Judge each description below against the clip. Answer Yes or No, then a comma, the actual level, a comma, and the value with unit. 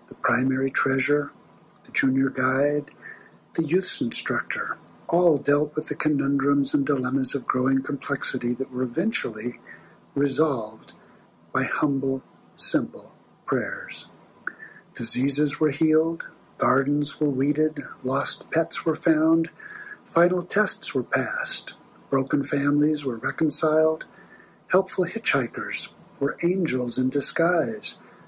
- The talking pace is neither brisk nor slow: No, slow, 110 wpm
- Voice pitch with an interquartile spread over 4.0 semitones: No, average, 2.9 semitones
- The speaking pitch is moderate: Yes, medium, 145 Hz